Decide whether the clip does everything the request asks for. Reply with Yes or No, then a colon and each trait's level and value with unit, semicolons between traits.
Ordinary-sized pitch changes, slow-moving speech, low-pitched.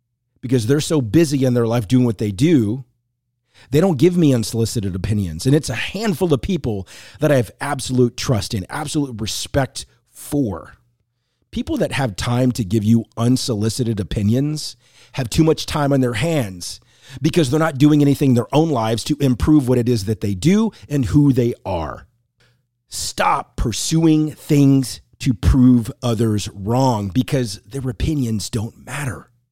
No: average, 4.0 semitones; average, 165 wpm; low, 125 Hz